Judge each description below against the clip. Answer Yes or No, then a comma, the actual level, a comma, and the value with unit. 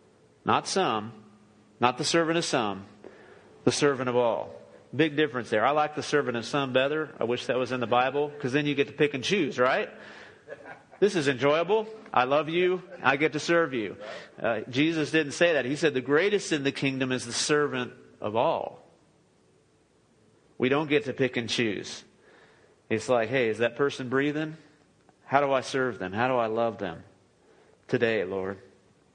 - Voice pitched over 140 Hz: No, low, 135 Hz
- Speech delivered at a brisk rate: No, average, 185 wpm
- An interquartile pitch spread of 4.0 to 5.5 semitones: Yes, average, 4.6 semitones